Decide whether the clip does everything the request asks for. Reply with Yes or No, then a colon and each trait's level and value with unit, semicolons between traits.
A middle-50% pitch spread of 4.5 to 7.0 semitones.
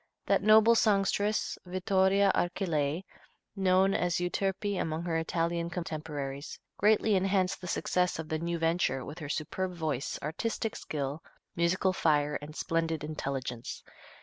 No: average, 3.6 semitones